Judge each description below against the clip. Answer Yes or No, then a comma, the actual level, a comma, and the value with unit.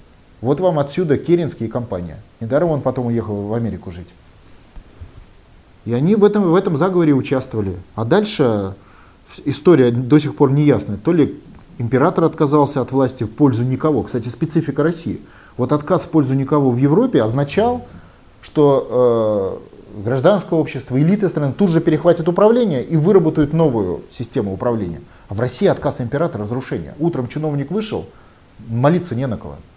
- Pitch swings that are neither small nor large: No, wide, 6.6 semitones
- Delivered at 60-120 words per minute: No, average, 155 wpm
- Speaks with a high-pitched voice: No, low, 135 Hz